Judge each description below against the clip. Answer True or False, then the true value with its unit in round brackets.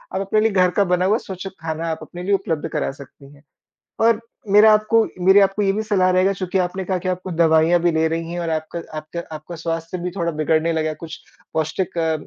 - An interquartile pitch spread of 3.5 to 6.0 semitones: False (3.1 semitones)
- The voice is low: False (175 Hz)